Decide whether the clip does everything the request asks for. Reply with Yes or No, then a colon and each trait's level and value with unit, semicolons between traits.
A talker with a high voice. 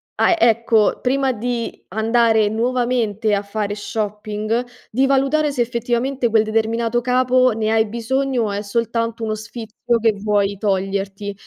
Yes: high, 225 Hz